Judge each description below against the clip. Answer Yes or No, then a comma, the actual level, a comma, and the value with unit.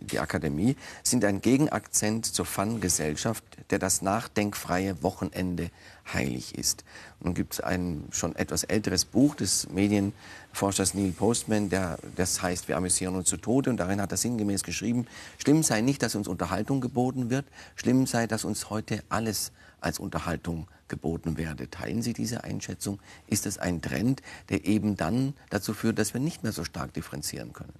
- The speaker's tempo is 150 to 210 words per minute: Yes, average, 170 wpm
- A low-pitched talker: Yes, low, 100 Hz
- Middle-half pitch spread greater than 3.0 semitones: Yes, average, 3.8 semitones